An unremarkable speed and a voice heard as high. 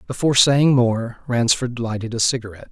No: average, 155 wpm; low, 120 Hz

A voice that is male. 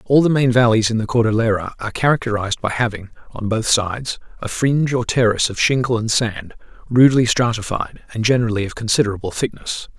Yes: male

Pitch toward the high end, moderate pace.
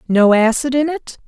Yes: very high, 255 Hz; average, 190 wpm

